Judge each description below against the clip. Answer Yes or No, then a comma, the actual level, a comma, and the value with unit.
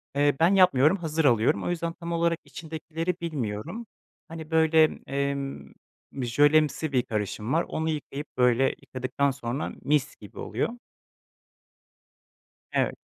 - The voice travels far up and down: No, average, 3.9 semitones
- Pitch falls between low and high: Yes, medium, 150 Hz